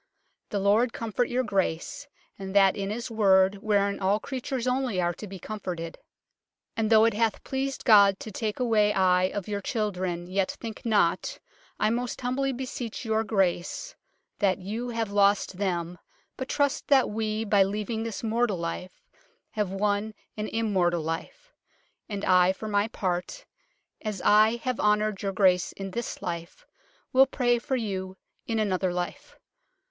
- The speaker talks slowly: No, average, 165 wpm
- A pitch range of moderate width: Yes, average, 3.3 semitones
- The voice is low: No, high, 210 Hz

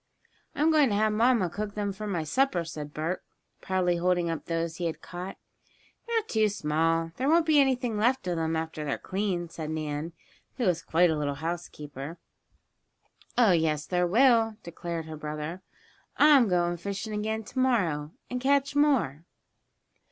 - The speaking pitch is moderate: Yes, medium, 180 Hz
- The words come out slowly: No, average, 165 wpm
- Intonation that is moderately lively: No, wide, 5.7 semitones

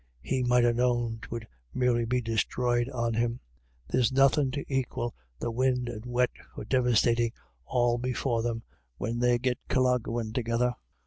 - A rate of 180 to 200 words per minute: No, average, 155 wpm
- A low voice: Yes, low, 120 Hz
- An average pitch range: No, narrow, 1.2 semitones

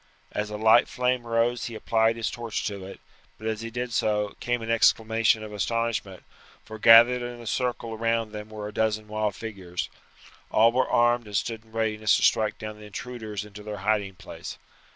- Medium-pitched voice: No, low, 110 Hz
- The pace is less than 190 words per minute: No, average, 195 wpm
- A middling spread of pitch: No, narrow, 1.6 semitones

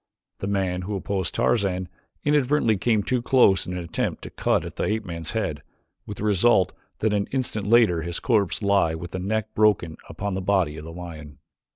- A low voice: Yes, low, 100 Hz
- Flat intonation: No, average, 3.6 semitones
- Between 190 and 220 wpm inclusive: Yes, average, 200 wpm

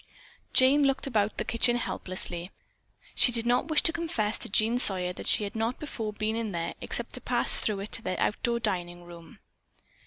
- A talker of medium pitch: No, high, 220 Hz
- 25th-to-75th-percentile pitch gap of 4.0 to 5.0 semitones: Yes, average, 4.6 semitones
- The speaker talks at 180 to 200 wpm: Yes, average, 195 wpm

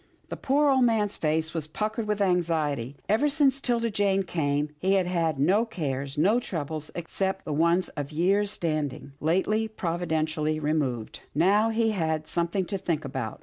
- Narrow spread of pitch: No, average, 5.2 semitones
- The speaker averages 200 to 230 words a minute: No, average, 170 wpm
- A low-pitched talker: No, medium, 170 Hz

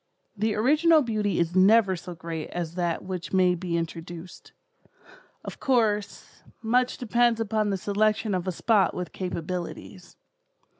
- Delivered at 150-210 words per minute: No, average, 140 wpm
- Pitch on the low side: No, high, 190 Hz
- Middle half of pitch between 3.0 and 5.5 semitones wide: Yes, average, 4.0 semitones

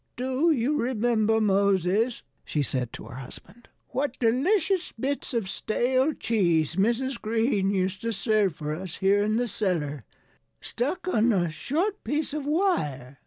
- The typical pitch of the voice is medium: No, high, 225 Hz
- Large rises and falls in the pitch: Yes, wide, 5.8 semitones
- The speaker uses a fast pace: No, average, 150 wpm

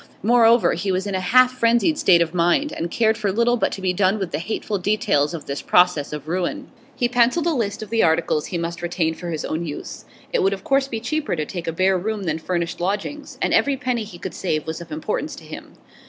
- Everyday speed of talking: No, fast, 245 wpm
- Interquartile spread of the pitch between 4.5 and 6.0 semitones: Yes, wide, 5.4 semitones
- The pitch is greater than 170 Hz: Yes, high, 190 Hz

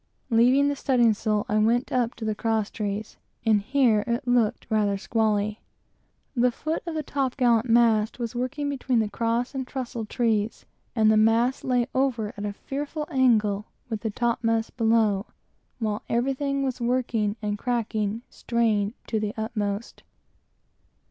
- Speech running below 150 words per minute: No, average, 160 wpm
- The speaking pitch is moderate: No, high, 230 Hz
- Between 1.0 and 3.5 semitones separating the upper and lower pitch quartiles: Yes, average, 2.7 semitones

